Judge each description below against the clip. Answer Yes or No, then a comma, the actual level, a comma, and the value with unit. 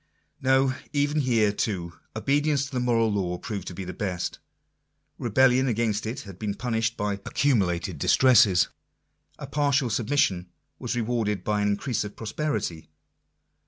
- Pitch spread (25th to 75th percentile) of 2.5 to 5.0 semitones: Yes, average, 4.6 semitones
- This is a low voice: Yes, low, 110 Hz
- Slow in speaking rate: No, average, 145 wpm